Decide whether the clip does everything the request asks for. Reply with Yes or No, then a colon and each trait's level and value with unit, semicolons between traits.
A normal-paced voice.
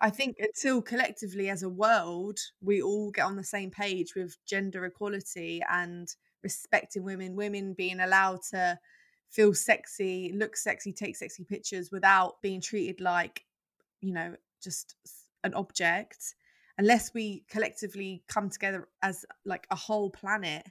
Yes: average, 145 wpm